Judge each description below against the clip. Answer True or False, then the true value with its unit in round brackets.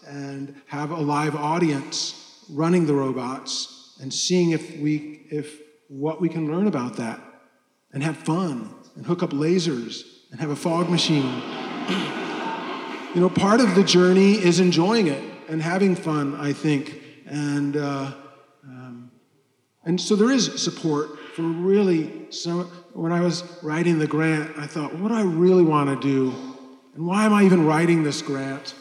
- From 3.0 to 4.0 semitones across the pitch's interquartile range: True (3.7 semitones)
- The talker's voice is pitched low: False (155 Hz)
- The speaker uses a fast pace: False (165 wpm)